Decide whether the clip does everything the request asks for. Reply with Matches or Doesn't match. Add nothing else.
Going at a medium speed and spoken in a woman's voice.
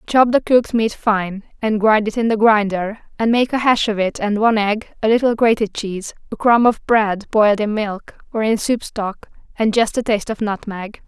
Doesn't match